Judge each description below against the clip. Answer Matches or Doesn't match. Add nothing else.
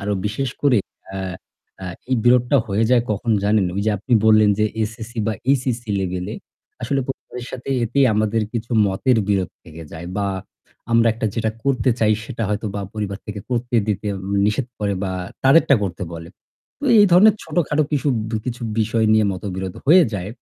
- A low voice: Matches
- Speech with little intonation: Doesn't match